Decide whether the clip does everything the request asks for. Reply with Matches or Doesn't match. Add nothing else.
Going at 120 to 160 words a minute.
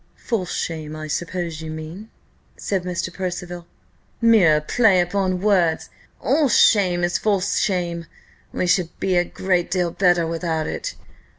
Matches